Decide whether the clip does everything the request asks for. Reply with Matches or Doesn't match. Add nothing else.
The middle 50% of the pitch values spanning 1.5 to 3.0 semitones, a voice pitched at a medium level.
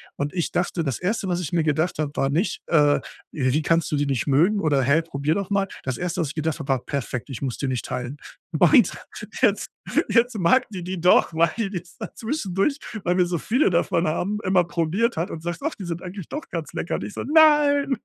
Doesn't match